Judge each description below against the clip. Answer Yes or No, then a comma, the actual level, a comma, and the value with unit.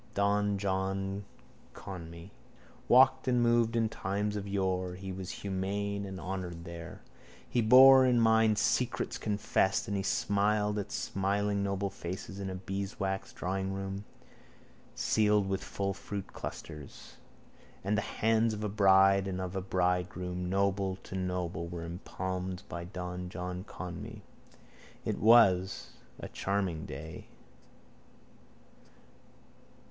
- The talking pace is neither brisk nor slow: No, slow, 125 wpm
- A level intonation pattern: Yes, narrow, 1.9 semitones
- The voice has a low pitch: Yes, very low, 95 Hz